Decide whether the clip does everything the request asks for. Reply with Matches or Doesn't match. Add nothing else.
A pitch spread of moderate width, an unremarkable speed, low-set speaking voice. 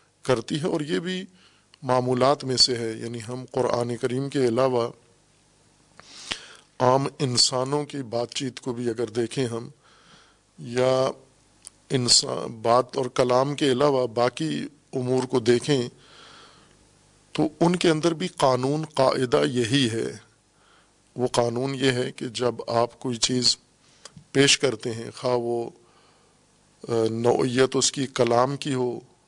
Doesn't match